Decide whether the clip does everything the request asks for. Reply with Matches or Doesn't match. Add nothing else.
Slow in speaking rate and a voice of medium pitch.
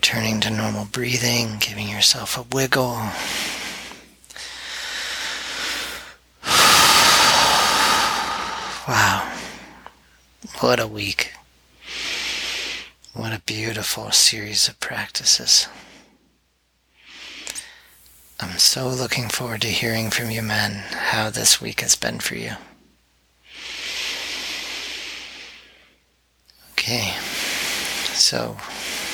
Doesn't match